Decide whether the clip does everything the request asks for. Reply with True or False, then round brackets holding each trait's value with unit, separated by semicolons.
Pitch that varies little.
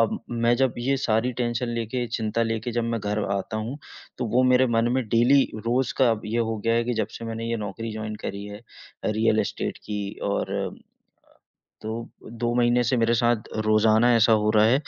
True (1.7 semitones)